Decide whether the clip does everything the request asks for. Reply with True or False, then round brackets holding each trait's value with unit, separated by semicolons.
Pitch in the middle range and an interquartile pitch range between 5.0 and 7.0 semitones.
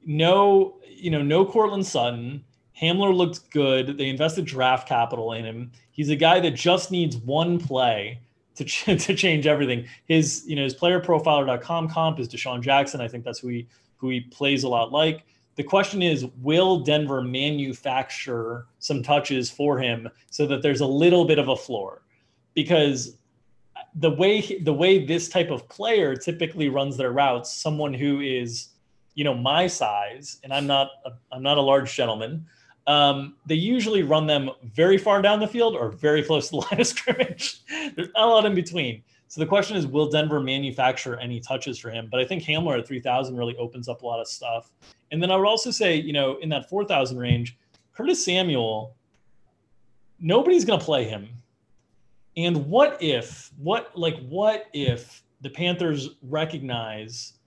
True (145 Hz; 5.4 semitones)